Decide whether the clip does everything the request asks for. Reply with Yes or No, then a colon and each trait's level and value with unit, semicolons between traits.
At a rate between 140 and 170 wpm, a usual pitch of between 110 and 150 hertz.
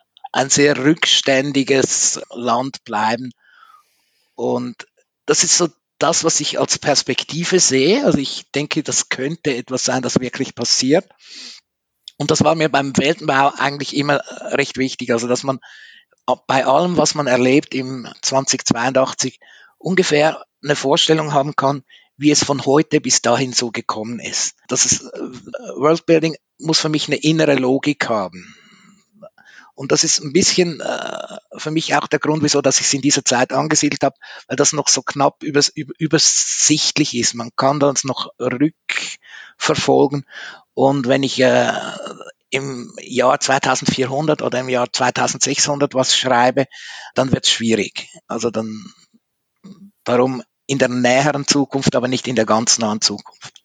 Yes: average, 150 wpm; medium, 140 Hz